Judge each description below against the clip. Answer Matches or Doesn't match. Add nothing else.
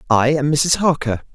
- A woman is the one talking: Doesn't match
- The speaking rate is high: Doesn't match